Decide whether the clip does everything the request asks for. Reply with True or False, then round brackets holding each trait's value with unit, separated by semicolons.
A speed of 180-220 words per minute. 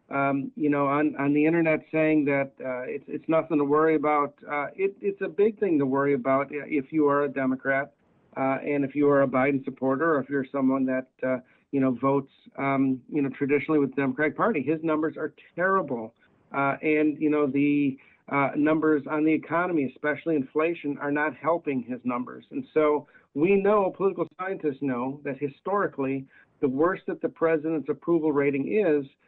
True (190 wpm)